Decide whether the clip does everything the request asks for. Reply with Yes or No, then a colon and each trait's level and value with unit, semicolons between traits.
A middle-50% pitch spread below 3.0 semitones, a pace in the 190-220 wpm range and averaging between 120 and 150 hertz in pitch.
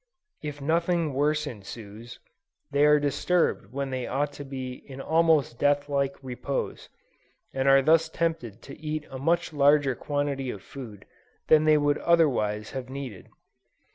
No: narrow, 2.6 semitones; average, 150 wpm; medium, 140 Hz